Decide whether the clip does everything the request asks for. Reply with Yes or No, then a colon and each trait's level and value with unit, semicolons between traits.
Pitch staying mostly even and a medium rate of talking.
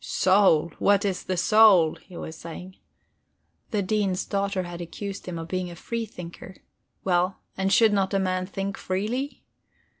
Yes: narrow, 2.2 semitones; average, 160 wpm